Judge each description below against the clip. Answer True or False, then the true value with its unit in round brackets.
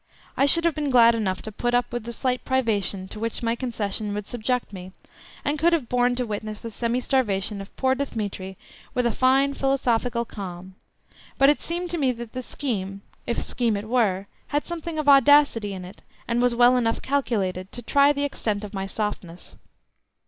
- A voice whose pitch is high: True (235 Hz)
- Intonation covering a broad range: False (4.3 semitones)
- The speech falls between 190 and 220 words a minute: True (200 wpm)